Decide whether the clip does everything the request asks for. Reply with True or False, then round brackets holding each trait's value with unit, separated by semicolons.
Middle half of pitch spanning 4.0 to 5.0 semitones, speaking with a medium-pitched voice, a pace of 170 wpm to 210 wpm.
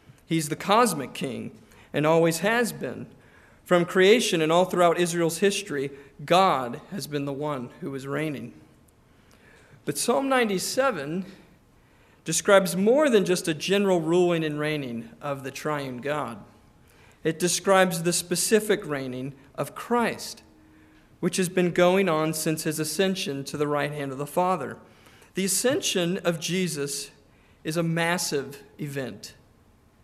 False (4.5 semitones; 170 Hz; 140 wpm)